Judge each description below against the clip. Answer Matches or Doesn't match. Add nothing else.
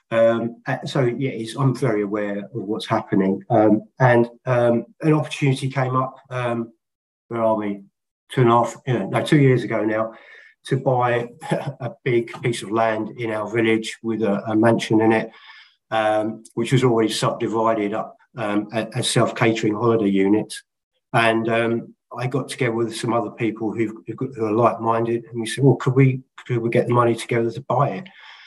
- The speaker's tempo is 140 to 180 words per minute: Doesn't match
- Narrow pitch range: Matches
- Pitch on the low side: Matches